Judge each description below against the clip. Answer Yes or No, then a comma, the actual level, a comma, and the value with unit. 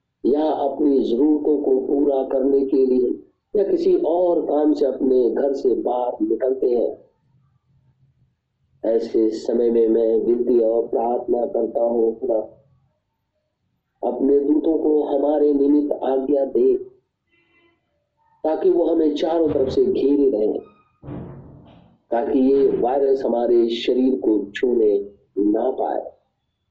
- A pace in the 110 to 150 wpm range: Yes, average, 120 wpm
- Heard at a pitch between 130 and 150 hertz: Yes, medium, 140 Hz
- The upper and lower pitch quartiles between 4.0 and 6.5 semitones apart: Yes, average, 5.2 semitones